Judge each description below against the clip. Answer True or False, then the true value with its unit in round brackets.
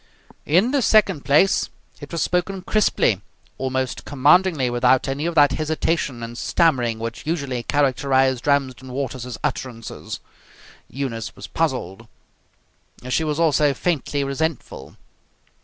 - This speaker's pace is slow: True (120 wpm)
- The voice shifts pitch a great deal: False (4.1 semitones)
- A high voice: False (140 Hz)